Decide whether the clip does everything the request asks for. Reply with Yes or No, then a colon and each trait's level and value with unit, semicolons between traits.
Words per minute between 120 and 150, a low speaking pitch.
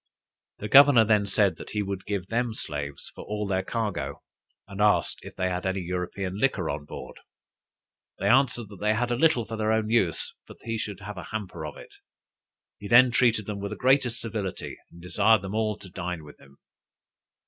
No: fast, 205 wpm; low, 105 Hz